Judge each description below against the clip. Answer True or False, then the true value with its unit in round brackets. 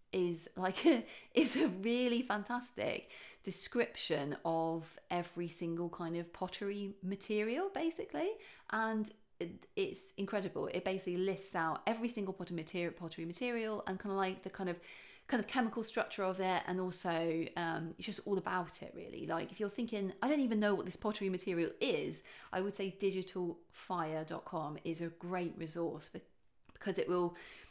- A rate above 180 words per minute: False (165 wpm)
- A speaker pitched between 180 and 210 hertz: True (190 Hz)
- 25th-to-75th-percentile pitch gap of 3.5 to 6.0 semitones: True (4.1 semitones)